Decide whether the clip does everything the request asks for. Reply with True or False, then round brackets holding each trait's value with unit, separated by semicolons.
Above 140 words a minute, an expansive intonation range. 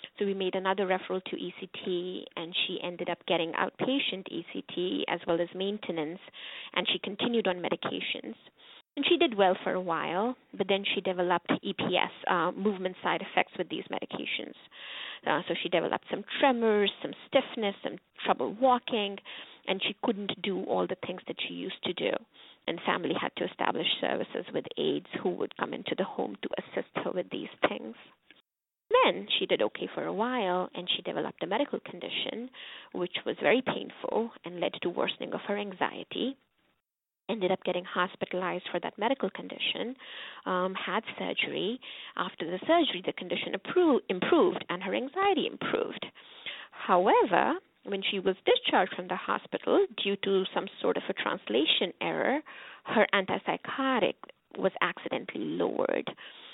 True (160 wpm; 6.1 semitones)